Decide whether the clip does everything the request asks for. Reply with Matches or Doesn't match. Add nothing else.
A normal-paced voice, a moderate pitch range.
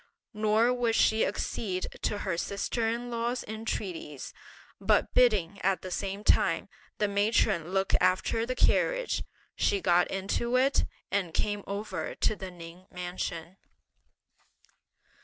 Doesn't match